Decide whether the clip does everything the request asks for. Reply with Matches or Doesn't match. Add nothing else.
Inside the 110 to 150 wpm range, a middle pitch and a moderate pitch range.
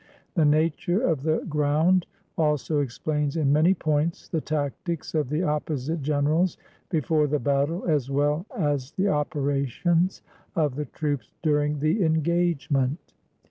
Doesn't match